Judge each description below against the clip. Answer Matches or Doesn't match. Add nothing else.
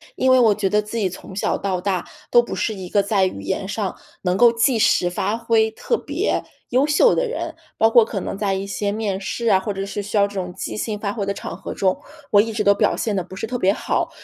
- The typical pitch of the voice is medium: Doesn't match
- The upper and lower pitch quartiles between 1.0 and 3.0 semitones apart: Matches